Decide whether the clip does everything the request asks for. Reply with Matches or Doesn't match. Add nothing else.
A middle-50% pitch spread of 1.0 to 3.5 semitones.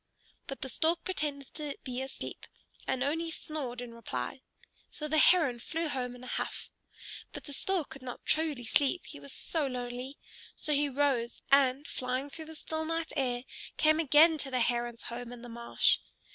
Doesn't match